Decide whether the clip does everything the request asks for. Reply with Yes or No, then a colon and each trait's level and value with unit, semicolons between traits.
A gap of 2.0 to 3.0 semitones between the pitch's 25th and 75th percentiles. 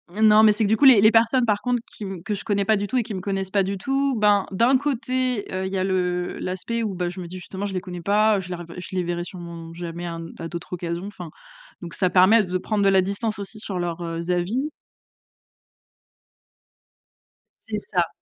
No: average, 3.4 semitones